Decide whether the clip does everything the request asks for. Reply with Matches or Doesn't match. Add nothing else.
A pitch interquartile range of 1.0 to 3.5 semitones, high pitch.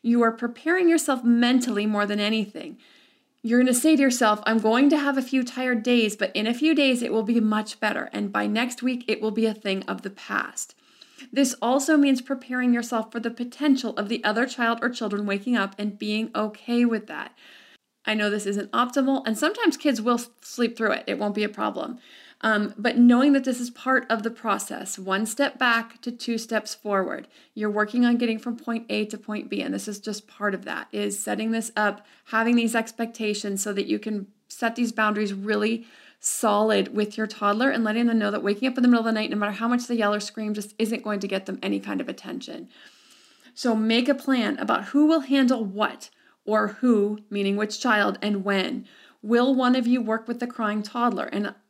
Matches